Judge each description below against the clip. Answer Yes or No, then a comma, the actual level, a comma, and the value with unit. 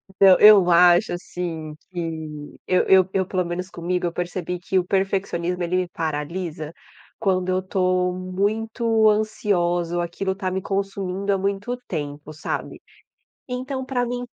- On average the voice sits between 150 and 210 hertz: Yes, medium, 185 Hz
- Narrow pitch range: Yes, narrow, 2.3 semitones